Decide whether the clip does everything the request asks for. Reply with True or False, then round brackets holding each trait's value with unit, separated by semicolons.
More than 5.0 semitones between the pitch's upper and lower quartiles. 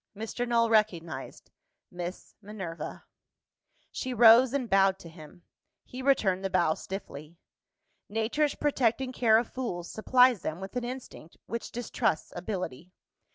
True (5.5 semitones)